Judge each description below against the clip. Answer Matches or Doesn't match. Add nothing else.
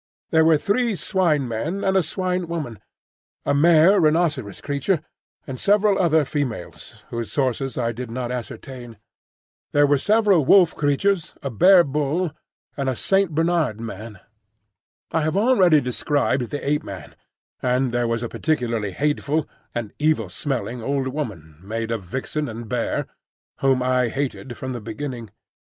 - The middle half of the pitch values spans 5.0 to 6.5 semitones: Matches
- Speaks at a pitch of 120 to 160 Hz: Matches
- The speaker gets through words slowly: Doesn't match